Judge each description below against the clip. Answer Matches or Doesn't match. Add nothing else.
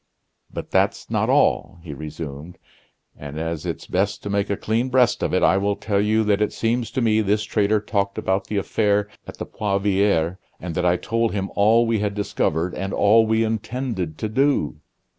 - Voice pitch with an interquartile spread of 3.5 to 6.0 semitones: Doesn't match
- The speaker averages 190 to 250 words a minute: Matches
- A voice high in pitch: Doesn't match